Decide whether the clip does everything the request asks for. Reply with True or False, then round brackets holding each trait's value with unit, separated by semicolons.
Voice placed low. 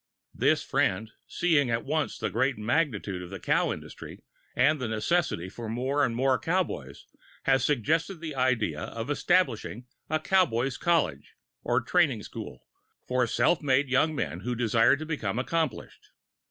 True (130 Hz)